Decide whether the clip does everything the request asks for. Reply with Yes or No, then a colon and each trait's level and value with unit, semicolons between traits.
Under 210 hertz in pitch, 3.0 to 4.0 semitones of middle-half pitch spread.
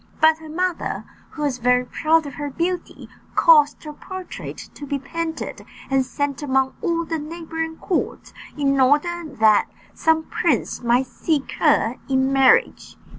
No: very high, 295 Hz; average, 3.5 semitones